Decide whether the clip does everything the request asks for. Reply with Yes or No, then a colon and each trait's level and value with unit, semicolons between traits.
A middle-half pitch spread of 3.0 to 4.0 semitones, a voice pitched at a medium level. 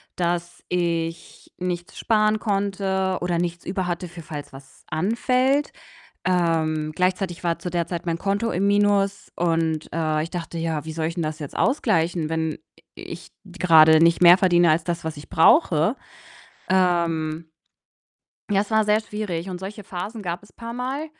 Yes: average, 3.3 semitones; medium, 175 Hz